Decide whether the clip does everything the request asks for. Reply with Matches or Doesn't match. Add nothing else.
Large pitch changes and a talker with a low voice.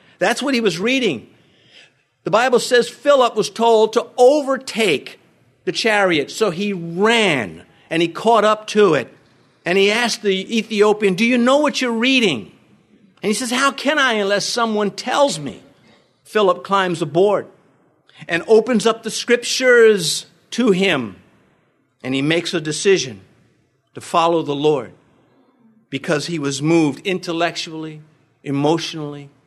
Doesn't match